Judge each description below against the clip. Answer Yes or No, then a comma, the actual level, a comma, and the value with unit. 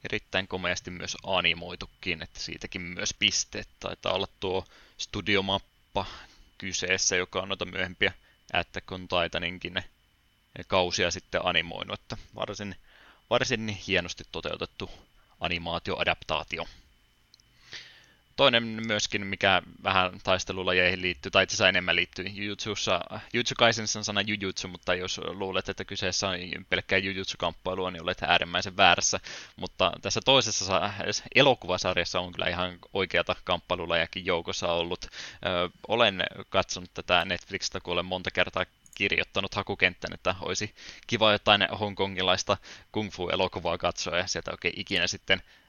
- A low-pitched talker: Yes, very low, 95 Hz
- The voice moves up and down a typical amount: No, narrow, 2.3 semitones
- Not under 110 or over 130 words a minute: Yes, average, 120 wpm